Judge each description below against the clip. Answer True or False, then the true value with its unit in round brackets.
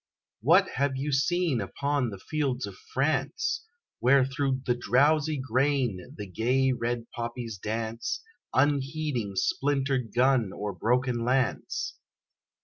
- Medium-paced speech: False (120 wpm)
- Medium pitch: False (130 Hz)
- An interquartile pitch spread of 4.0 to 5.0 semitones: False (3.3 semitones)